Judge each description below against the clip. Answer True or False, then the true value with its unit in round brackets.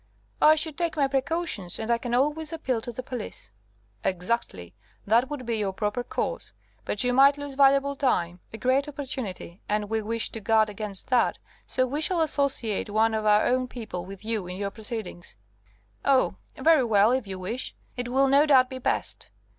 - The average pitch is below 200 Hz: False (245 Hz)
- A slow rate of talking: False (190 wpm)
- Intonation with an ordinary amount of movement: True (4.6 semitones)